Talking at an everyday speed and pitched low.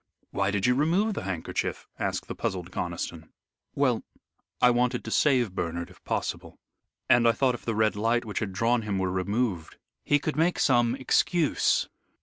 Yes: average, 175 wpm; low, 115 Hz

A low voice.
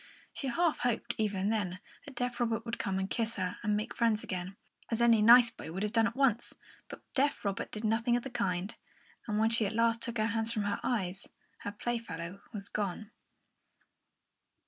No: high, 225 Hz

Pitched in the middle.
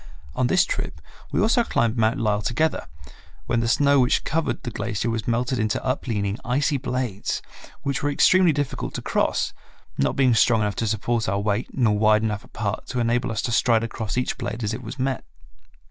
No: low, 120 Hz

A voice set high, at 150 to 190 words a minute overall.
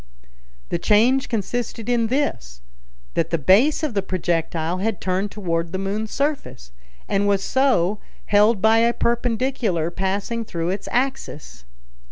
No: high, 205 Hz; average, 140 wpm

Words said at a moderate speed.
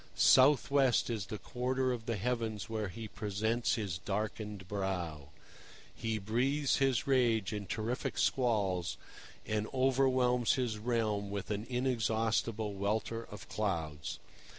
No: slow, 130 wpm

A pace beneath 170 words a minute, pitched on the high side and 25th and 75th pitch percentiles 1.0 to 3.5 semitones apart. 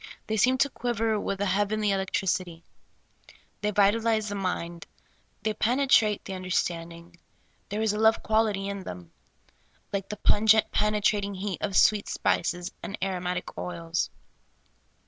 Yes: average, 145 wpm; high, 200 Hz; average, 2.9 semitones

